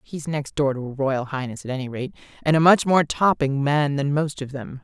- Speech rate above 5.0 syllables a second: Yes, 5.2 syllables/s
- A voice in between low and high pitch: Yes, medium, 145 Hz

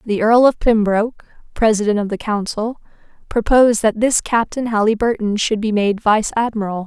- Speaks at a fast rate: No, average, 155 wpm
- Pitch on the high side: Yes, high, 220 Hz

